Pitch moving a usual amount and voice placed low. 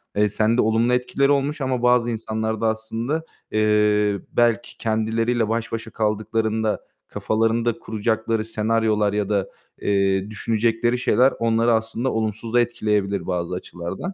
No: narrow, 1.7 semitones; low, 110 Hz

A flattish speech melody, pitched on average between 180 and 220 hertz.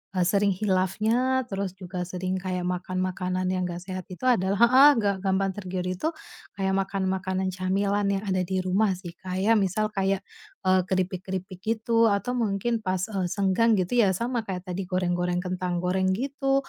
Yes: narrow, 2.0 semitones; high, 190 Hz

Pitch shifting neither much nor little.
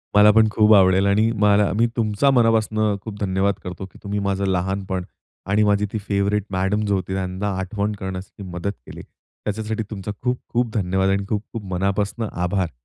No: narrow, 2.0 semitones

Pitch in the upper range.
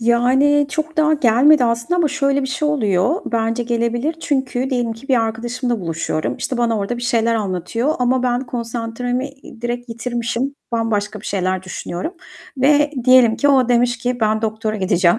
Yes: high, 240 Hz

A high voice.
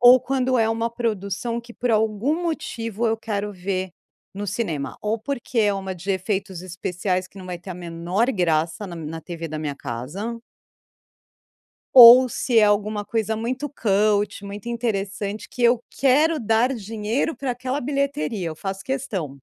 Yes: high, 210 Hz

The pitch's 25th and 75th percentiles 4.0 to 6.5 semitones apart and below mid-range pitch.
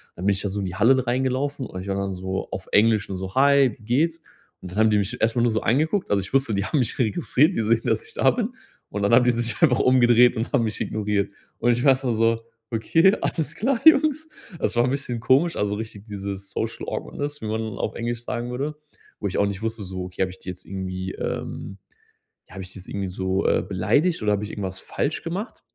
Yes: average, 5.1 semitones; low, 115 Hz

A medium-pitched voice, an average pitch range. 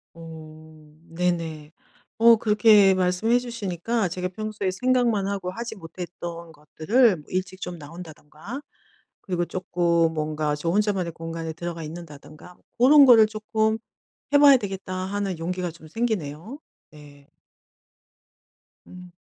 Yes: medium, 180 Hz; average, 4.7 semitones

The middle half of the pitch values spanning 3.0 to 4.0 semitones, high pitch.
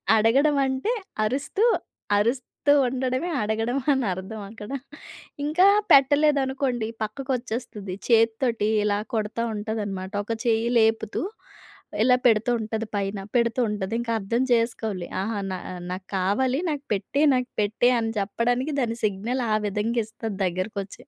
Yes: average, 3.5 semitones; high, 225 Hz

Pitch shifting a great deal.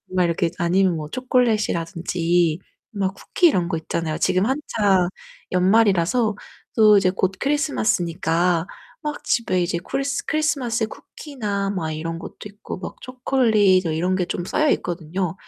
No: average, 4.7 semitones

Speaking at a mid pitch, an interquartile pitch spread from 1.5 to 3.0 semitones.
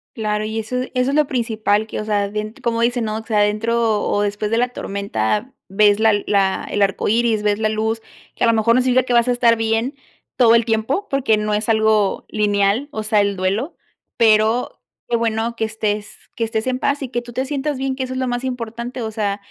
No: high, 225 Hz; narrow, 2.4 semitones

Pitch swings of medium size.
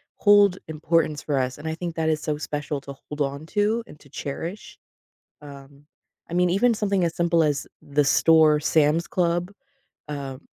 Yes: average, 3.1 semitones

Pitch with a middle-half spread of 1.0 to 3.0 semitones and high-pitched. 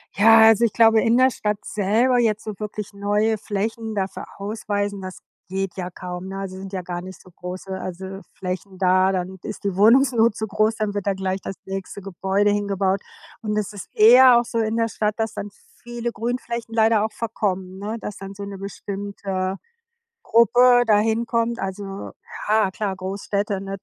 Yes: narrow, 2.6 semitones; high, 205 Hz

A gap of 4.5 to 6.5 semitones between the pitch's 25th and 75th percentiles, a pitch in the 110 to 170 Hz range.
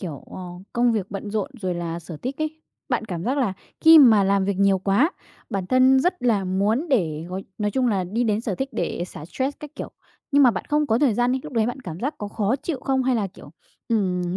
No: wide, 5.5 semitones; high, 220 Hz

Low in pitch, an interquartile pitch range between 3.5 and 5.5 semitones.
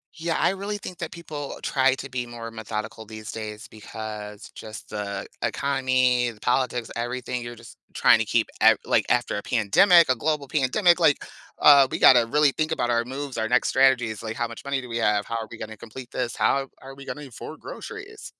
Yes: low, 125 Hz; average, 3.9 semitones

